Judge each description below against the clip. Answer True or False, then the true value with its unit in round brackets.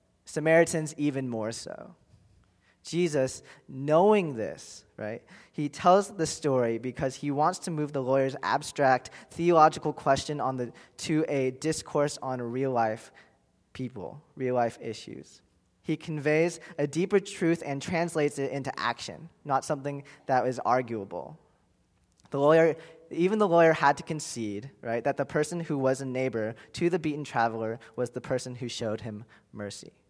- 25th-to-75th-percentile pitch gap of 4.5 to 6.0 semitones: True (4.8 semitones)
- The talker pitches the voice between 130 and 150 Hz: True (140 Hz)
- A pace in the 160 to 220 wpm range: False (150 wpm)